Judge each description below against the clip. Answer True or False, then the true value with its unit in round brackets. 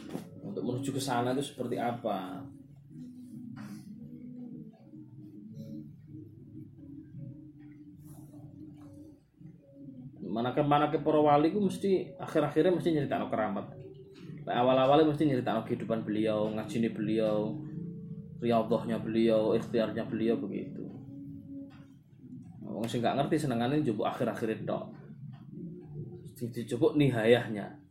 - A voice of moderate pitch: True (145 Hz)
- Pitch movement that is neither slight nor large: True (4.1 semitones)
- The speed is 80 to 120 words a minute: True (90 wpm)